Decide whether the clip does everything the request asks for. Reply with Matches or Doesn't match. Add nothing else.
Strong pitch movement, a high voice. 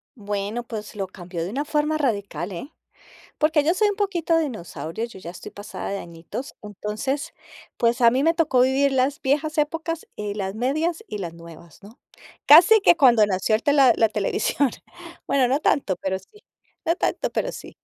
Matches